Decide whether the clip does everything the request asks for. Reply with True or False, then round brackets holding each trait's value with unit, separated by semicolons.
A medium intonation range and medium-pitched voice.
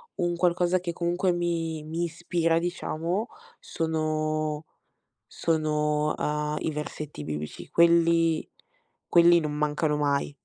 False (2.2 semitones; 160 Hz)